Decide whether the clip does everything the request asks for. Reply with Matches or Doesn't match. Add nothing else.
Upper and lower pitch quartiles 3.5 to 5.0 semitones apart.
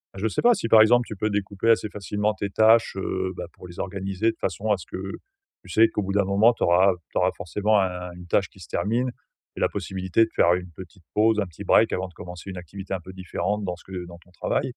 Doesn't match